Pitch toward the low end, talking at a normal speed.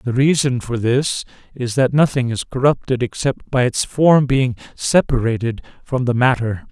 Yes: low, 125 Hz; average, 160 wpm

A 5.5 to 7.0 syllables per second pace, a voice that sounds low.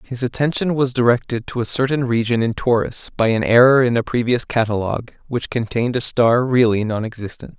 Yes: 5.6 syllables/s; low, 120 Hz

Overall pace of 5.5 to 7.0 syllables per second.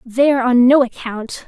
No: 4.4 syllables/s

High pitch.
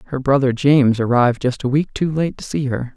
No: low, 135 Hz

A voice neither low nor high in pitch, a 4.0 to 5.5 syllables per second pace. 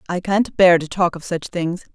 Yes: medium, 180 Hz; 5.0 syllables/s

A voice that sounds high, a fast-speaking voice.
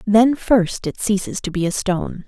Yes: high, 200 Hz; fast, 210 wpm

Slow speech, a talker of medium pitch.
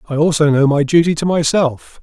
No: fast, 205 wpm; medium, 155 Hz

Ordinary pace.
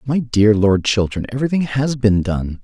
Yes: average, 180 wpm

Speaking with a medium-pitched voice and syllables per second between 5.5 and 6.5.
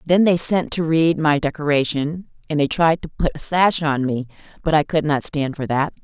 No: medium, 155 Hz; 5.0 syllables/s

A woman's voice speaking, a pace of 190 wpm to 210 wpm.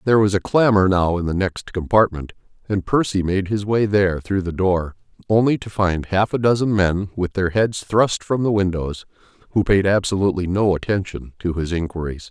No: male; average, 195 wpm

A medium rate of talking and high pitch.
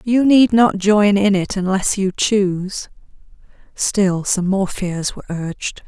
Yes: average, 155 wpm; high, 195 Hz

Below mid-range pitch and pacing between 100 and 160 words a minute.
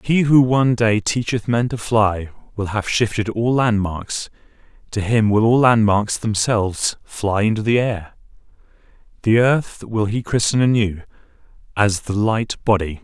Yes: low, 110 Hz; average, 145 wpm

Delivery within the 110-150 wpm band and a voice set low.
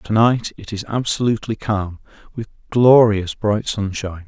Yes: average, 140 wpm; low, 110 Hz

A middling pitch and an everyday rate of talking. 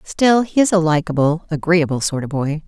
Yes: medium, 165 Hz; average, 180 wpm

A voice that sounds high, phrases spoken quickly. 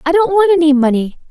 Yes: very high, 320 Hz; fast, 230 wpm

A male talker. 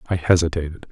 Yes: male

